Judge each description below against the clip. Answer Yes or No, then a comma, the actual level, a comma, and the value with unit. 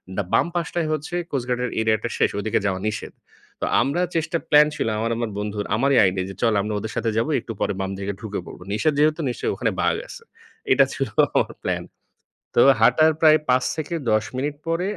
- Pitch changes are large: Yes, wide, 6.4 semitones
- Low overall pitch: Yes, low, 120 Hz